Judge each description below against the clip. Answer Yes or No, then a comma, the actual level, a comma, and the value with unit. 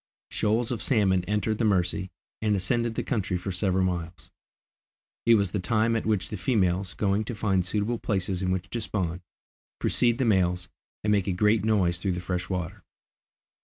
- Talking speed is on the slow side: No, average, 185 wpm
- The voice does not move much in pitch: No, average, 3.1 semitones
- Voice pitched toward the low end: Yes, low, 100 Hz